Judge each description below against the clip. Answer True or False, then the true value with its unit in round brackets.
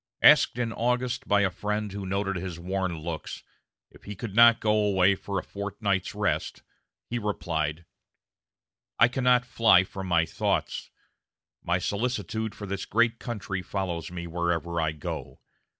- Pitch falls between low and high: False (100 Hz)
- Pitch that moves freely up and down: False (3.8 semitones)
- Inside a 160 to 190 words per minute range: False (150 wpm)